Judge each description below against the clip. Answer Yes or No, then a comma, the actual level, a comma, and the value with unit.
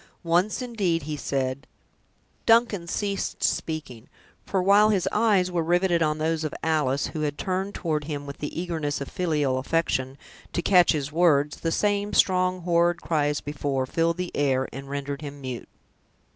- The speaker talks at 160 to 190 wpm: Yes, average, 170 wpm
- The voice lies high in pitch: No, medium, 160 Hz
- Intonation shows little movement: No, average, 4.1 semitones